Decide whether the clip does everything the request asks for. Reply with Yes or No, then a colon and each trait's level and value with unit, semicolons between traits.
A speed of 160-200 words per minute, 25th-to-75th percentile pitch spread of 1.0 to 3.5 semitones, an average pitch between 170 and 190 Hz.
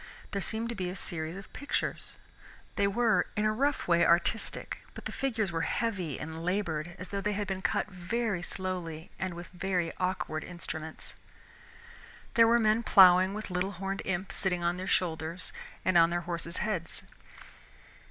Yes: average, 170 wpm; average, 3.2 semitones; medium, 185 Hz